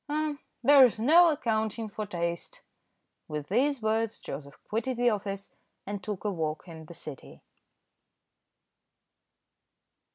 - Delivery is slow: Yes, slow, 120 wpm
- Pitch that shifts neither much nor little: No, wide, 6.1 semitones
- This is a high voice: Yes, high, 215 Hz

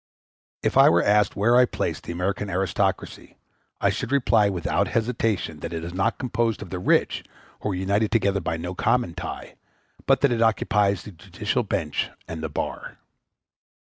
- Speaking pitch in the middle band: No, low, 100 Hz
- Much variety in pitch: No, average, 4.2 semitones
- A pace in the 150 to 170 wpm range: No, average, 180 wpm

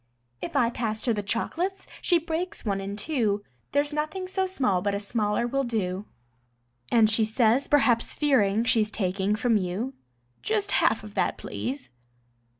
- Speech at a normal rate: Yes, average, 160 wpm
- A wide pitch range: Yes, wide, 5.9 semitones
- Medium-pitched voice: No, high, 230 Hz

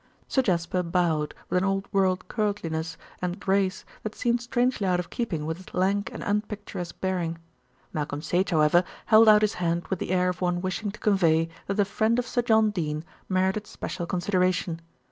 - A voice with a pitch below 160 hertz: No, medium, 185 Hz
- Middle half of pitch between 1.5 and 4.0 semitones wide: Yes, average, 3.3 semitones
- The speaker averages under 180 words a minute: No, average, 185 wpm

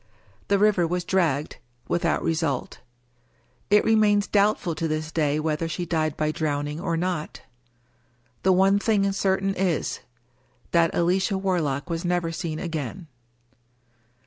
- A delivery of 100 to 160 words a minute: Yes, average, 140 wpm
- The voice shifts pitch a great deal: No, average, 3.6 semitones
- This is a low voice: No, medium, 170 Hz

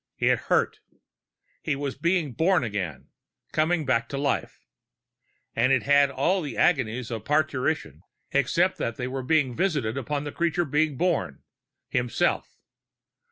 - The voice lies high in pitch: No, medium, 140 Hz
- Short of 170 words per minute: Yes, slow, 135 wpm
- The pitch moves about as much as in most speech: Yes, average, 4.2 semitones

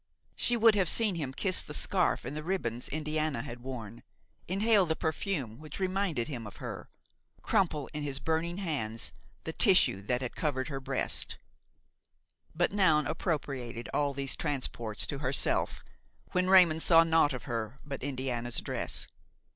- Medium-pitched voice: Yes, medium, 150 Hz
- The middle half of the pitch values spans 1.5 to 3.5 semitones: No, average, 5.2 semitones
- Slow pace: No, average, 155 wpm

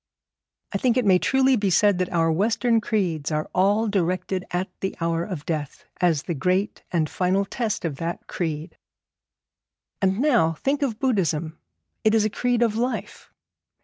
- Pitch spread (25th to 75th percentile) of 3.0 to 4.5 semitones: No, average, 5.0 semitones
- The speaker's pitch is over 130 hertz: Yes, high, 190 Hz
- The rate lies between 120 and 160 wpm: No, average, 170 wpm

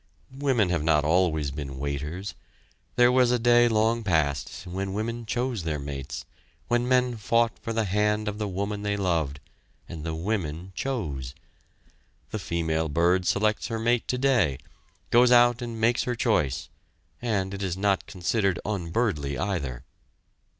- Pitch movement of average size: No, wide, 6.4 semitones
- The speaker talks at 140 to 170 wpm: Yes, average, 150 wpm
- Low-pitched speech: Yes, low, 100 Hz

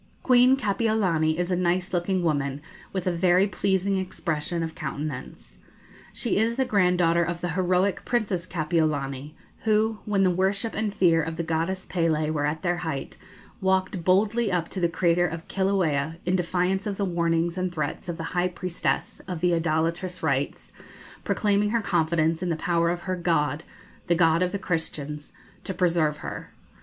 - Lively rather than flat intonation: No, narrow, 2.6 semitones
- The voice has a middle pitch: Yes, medium, 175 Hz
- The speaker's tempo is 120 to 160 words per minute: No, average, 170 wpm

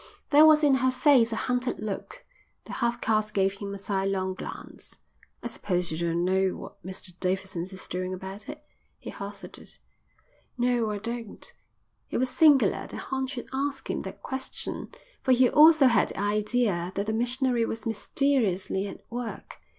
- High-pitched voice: Yes, high, 225 Hz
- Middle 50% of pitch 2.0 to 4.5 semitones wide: No, average, 5.1 semitones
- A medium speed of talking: Yes, average, 170 wpm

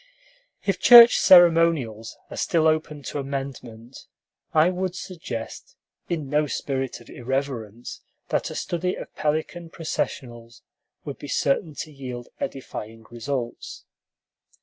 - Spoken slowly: Yes, slow, 120 wpm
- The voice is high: No, medium, 140 Hz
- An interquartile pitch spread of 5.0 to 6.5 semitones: Yes, average, 5.3 semitones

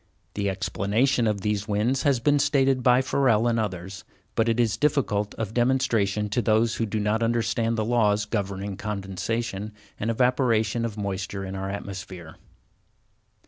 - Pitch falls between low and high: No, low, 110 Hz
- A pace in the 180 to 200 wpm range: No, average, 155 wpm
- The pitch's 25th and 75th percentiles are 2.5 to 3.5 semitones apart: Yes, average, 3.0 semitones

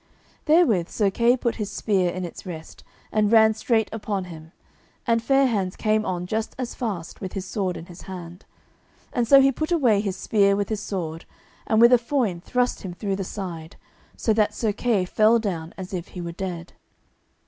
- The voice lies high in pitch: Yes, high, 205 Hz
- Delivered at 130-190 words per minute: No, average, 200 wpm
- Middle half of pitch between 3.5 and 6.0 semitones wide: Yes, average, 4.1 semitones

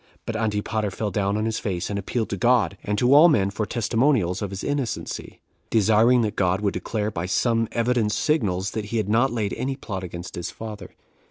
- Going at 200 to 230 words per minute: Yes, fast, 205 wpm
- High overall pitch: No, low, 110 Hz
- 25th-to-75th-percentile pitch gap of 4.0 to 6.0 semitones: No, average, 2.9 semitones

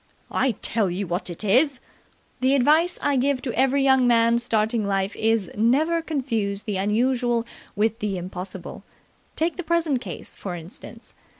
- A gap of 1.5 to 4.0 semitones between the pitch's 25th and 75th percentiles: No, average, 5.1 semitones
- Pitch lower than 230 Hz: No, high, 235 Hz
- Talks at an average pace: Yes, average, 165 wpm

